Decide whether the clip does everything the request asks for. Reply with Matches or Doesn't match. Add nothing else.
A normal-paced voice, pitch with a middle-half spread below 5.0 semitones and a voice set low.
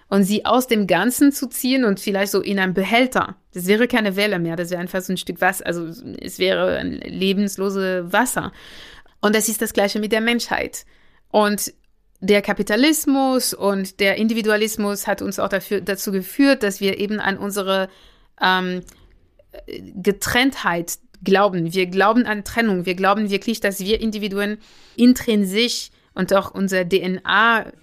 Doesn't match